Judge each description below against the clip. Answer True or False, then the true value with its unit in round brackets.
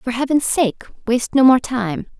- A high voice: True (245 Hz)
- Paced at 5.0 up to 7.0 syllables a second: False (4.6 syllables/s)